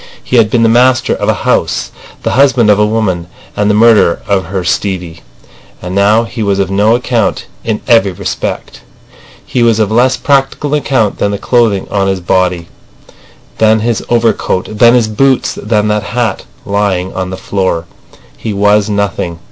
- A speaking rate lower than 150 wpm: No, average, 170 wpm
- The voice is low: Yes, low, 105 Hz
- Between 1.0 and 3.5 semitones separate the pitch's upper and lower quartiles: Yes, average, 3.1 semitones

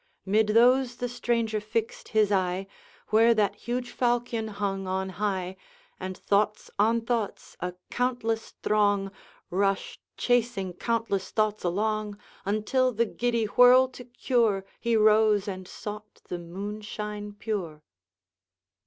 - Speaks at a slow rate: Yes, slow, 125 wpm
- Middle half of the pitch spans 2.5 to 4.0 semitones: Yes, average, 3.0 semitones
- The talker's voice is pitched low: No, high, 215 Hz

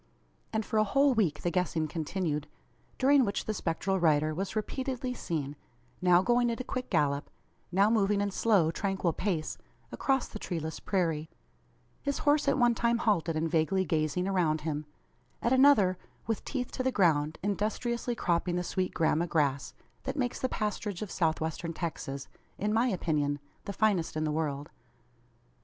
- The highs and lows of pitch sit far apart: Yes, wide, 5.9 semitones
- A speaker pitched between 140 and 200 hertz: Yes, medium, 185 Hz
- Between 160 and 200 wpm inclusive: Yes, average, 170 wpm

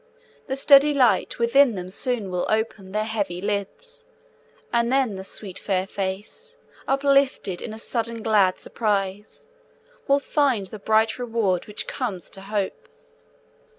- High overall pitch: Yes, high, 220 Hz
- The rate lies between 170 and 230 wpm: No, average, 140 wpm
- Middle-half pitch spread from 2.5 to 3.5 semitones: No, average, 4.7 semitones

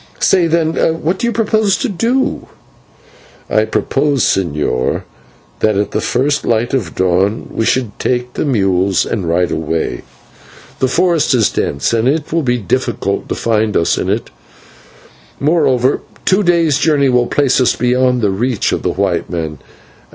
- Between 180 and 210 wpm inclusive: No, average, 160 wpm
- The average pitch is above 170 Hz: No, low, 125 Hz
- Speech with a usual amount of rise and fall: No, wide, 7.2 semitones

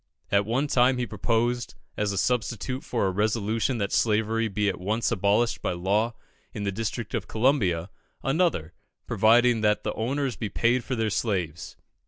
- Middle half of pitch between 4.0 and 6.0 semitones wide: No, average, 3.2 semitones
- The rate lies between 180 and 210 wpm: No, average, 170 wpm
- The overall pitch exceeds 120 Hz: No, low, 110 Hz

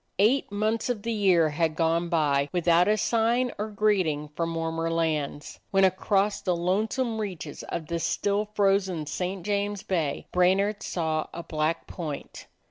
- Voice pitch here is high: No, medium, 180 Hz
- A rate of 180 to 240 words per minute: No, average, 160 wpm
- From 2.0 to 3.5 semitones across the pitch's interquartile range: No, average, 4.0 semitones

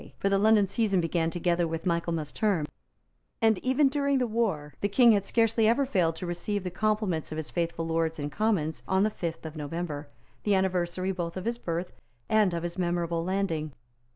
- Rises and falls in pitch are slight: No, average, 4.4 semitones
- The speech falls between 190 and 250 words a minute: Yes, average, 195 wpm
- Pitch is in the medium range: Yes, medium, 180 Hz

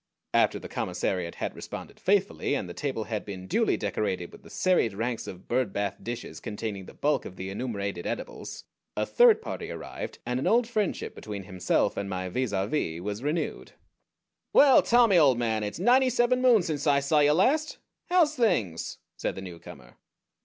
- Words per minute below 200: Yes, average, 185 wpm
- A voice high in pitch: No, low, 120 Hz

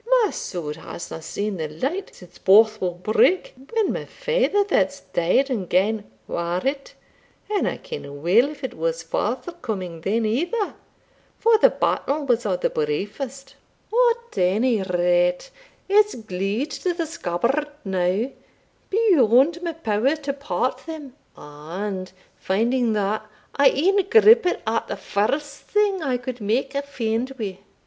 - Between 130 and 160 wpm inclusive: Yes, average, 140 wpm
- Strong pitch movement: Yes, wide, 8.3 semitones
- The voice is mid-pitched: No, high, 240 Hz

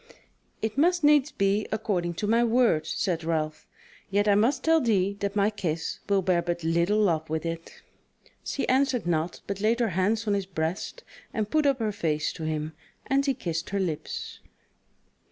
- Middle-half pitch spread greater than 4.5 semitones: Yes, average, 5.3 semitones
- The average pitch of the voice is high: Yes, high, 200 Hz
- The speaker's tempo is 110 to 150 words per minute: No, average, 185 wpm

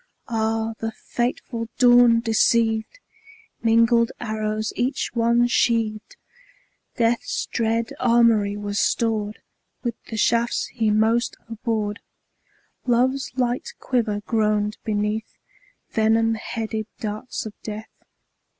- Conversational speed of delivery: No, slow, 100 wpm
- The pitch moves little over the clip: Yes, narrow, 1.5 semitones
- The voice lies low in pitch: No, high, 225 Hz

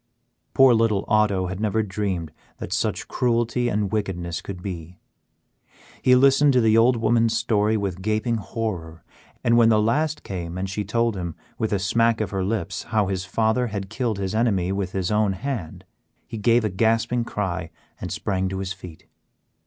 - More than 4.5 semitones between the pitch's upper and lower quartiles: No, average, 3.4 semitones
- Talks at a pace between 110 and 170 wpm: No, average, 180 wpm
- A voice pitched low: Yes, low, 105 Hz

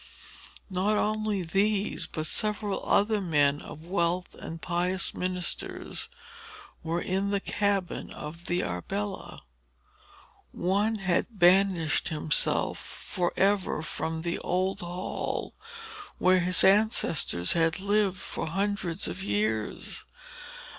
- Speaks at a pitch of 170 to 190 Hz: Yes, medium, 185 Hz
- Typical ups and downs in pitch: Yes, average, 3.3 semitones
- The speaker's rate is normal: No, slow, 110 wpm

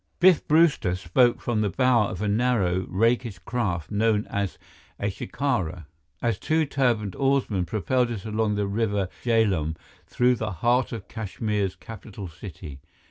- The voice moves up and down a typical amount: Yes, average, 4.2 semitones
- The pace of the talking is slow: No, average, 145 wpm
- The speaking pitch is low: Yes, low, 110 Hz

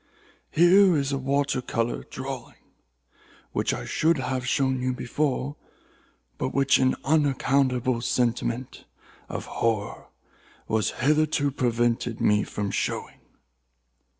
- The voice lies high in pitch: No, low, 130 Hz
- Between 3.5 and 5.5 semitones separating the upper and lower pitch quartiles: No, average, 2.7 semitones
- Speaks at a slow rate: Yes, slow, 105 wpm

